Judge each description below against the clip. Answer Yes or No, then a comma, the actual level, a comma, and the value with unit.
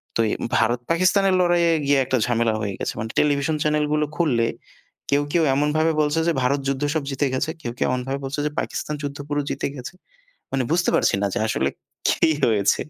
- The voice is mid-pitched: Yes, medium, 145 Hz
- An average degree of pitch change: Yes, average, 3.8 semitones